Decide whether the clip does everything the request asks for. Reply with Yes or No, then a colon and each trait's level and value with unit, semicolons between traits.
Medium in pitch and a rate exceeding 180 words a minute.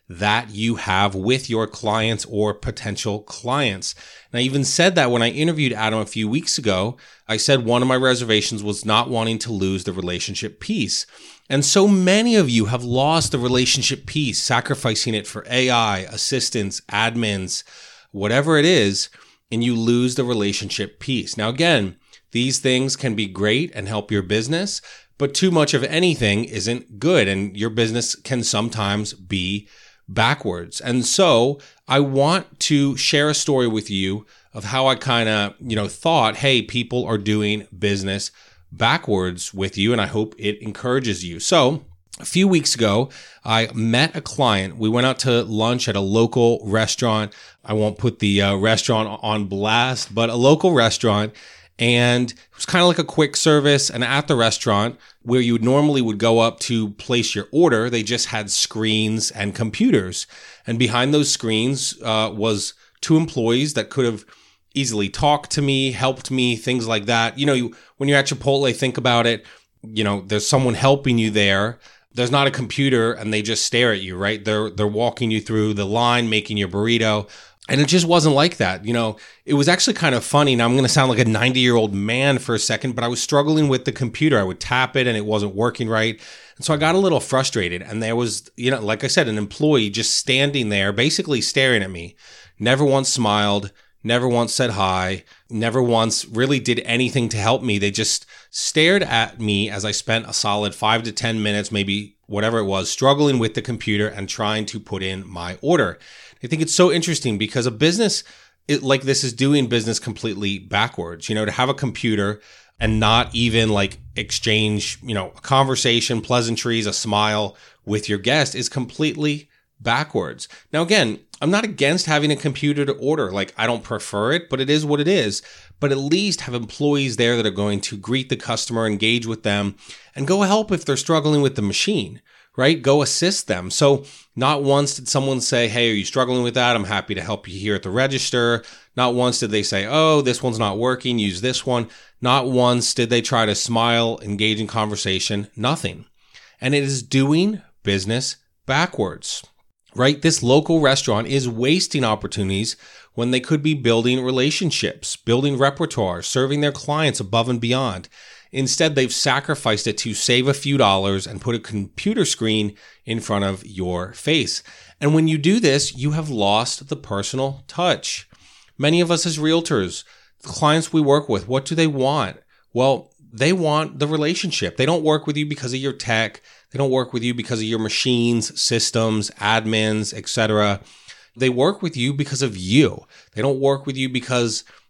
No: low, 120 Hz; average, 190 wpm